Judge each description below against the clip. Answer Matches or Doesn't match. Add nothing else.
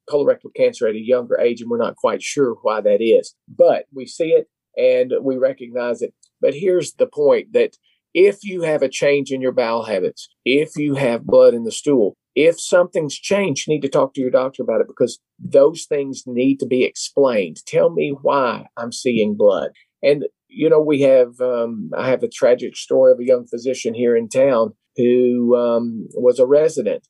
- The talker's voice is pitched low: Doesn't match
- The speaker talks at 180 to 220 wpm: Matches